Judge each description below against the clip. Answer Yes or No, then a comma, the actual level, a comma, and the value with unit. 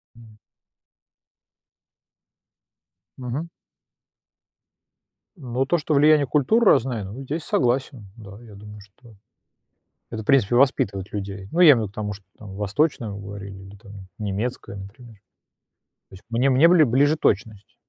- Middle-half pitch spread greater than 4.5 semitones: Yes, average, 5.2 semitones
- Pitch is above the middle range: No, low, 115 Hz